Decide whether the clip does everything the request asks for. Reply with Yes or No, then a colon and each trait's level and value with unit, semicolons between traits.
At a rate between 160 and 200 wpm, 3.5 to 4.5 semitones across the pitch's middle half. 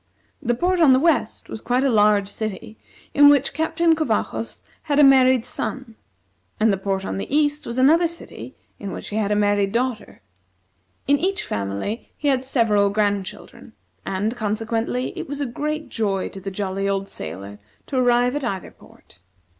No: average, 180 wpm; wide, 5.6 semitones